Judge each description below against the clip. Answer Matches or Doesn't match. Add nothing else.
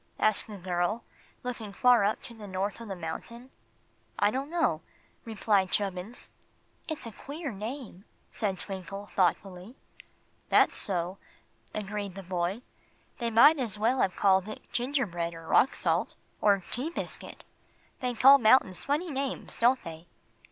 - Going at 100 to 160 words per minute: Matches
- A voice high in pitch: Matches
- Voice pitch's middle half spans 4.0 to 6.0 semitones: Matches